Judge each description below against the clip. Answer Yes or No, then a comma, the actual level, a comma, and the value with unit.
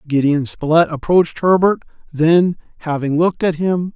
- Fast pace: No, slow, 135 wpm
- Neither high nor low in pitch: Yes, medium, 165 Hz